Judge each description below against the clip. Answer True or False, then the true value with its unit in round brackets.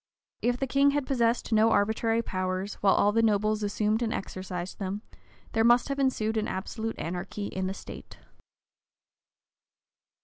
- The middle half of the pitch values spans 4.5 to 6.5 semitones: False (3.0 semitones)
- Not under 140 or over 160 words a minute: True (150 wpm)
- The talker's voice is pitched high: True (215 Hz)